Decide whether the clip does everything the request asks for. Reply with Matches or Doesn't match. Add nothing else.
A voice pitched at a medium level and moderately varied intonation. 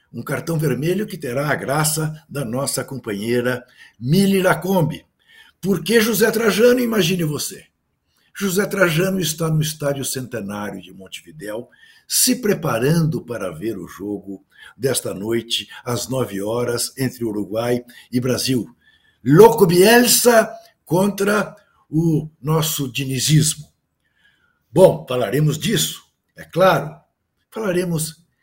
Doesn't match